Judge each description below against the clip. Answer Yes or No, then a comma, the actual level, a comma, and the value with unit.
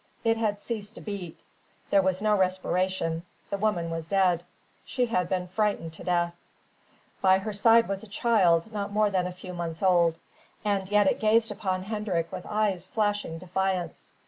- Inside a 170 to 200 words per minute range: Yes, average, 175 wpm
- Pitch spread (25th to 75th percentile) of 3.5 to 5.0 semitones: No, average, 2.9 semitones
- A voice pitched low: No, high, 190 Hz